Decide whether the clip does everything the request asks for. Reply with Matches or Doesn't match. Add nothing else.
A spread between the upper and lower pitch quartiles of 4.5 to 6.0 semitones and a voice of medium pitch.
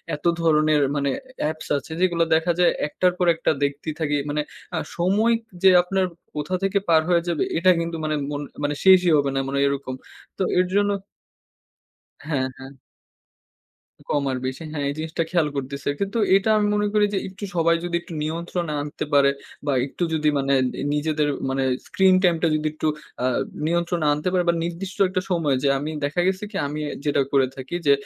Doesn't match